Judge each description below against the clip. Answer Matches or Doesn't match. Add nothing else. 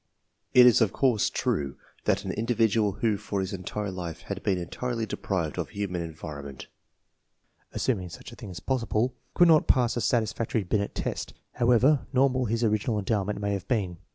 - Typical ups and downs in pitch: Matches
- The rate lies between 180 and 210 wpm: Matches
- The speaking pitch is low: Matches